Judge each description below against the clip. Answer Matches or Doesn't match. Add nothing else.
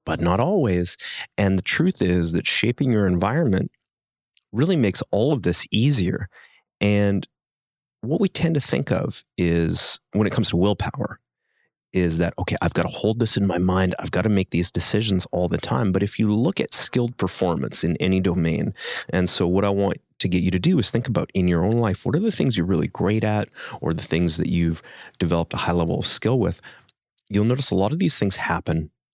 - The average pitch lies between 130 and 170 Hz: Doesn't match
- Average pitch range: Matches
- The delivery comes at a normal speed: Doesn't match